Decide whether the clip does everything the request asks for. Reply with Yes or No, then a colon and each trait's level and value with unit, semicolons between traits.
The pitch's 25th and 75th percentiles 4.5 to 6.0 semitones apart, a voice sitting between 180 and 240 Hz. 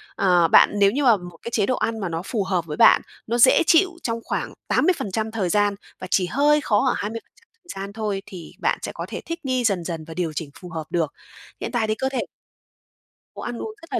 Yes: average, 5.2 semitones; high, 210 Hz